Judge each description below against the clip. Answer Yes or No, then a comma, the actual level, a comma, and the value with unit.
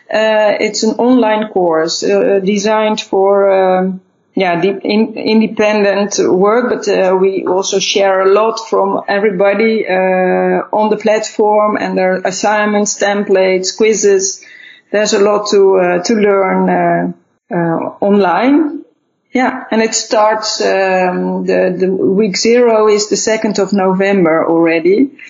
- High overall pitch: Yes, high, 200 Hz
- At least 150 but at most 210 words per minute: No, slow, 135 wpm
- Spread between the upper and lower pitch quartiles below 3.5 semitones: Yes, narrow, 2.5 semitones